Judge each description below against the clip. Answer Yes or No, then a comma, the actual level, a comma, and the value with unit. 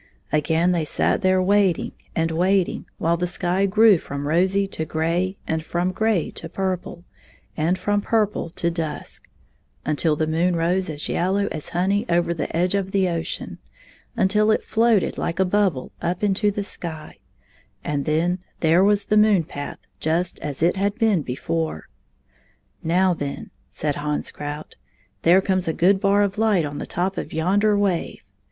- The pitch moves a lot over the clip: No, average, 3.5 semitones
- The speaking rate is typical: Yes, average, 175 wpm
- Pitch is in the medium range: Yes, medium, 180 Hz